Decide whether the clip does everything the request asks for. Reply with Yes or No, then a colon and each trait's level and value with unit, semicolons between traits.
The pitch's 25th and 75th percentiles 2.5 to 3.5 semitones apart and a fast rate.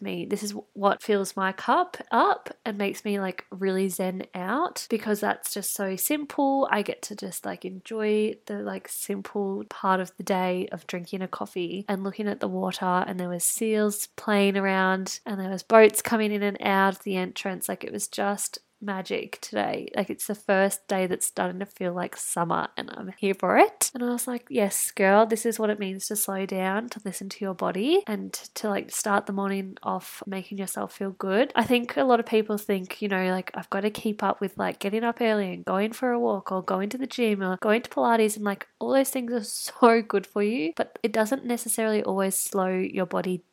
Yes: average, 2.8 semitones; fast, 225 wpm